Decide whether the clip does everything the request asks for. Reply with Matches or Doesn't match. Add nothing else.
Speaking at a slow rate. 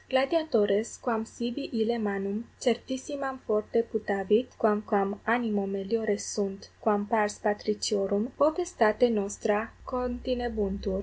Matches